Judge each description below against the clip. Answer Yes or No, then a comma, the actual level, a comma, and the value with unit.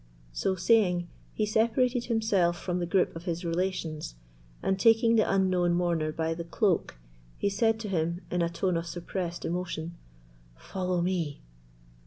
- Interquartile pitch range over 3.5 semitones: No, average, 2.8 semitones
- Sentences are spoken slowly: No, average, 155 wpm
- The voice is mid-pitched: Yes, medium, 180 Hz